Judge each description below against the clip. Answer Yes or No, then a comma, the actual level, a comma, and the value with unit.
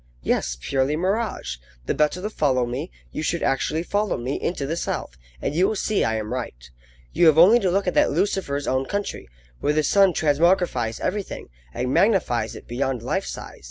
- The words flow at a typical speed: Yes, average, 195 wpm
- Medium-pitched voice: Yes, medium, 150 Hz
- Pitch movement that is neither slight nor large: No, wide, 6.7 semitones